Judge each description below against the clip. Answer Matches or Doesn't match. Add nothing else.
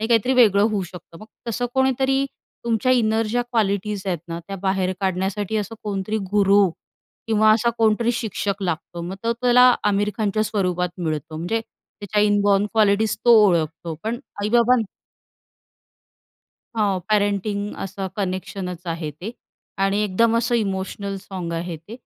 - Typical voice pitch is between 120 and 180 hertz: Doesn't match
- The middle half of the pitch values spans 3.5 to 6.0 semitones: Doesn't match